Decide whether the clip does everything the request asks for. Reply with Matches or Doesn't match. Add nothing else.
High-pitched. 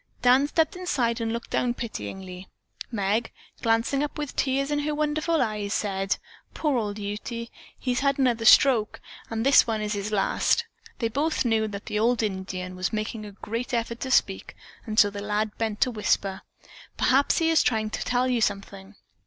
Matches